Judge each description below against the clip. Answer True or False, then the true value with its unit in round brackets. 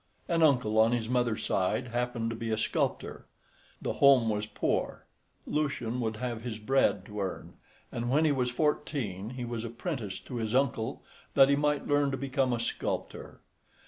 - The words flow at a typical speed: True (175 wpm)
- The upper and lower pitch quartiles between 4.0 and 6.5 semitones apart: False (3.5 semitones)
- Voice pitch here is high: False (120 Hz)